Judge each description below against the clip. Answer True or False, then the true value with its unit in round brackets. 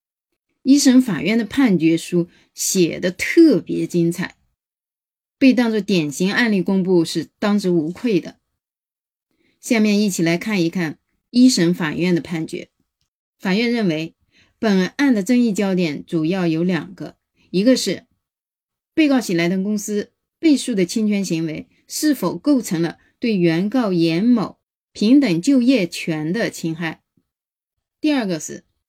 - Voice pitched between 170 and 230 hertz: True (185 Hz)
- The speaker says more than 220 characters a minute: False (205 characters per minute)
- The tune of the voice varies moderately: False (6.2 semitones)